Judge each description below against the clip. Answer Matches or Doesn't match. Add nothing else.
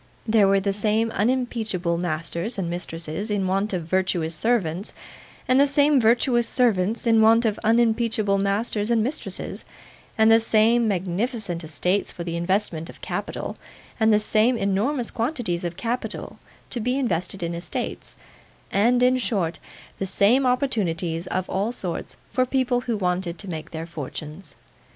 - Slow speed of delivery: Doesn't match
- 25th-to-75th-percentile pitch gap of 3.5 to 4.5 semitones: Doesn't match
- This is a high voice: Matches